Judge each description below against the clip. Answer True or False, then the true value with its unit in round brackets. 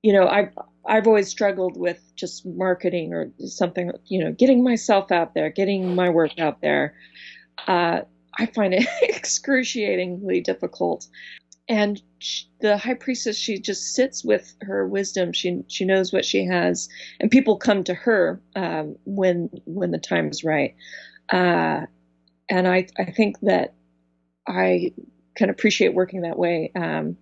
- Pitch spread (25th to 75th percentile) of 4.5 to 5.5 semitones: True (4.8 semitones)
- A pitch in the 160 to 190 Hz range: True (185 Hz)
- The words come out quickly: False (155 wpm)